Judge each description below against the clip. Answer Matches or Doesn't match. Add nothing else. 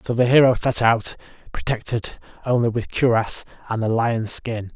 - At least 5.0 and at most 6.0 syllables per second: Doesn't match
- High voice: Doesn't match